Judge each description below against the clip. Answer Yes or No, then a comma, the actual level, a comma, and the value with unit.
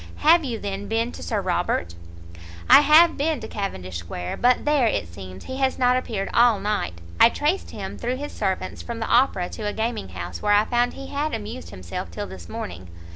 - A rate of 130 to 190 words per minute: No, fast, 205 wpm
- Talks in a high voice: Yes, high, 215 Hz